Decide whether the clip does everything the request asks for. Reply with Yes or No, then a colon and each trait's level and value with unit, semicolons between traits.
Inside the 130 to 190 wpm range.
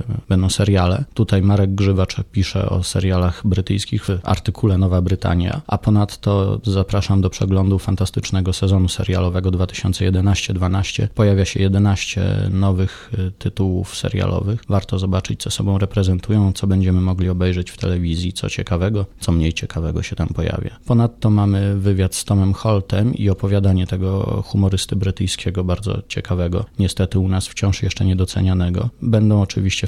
Yes: average, 135 wpm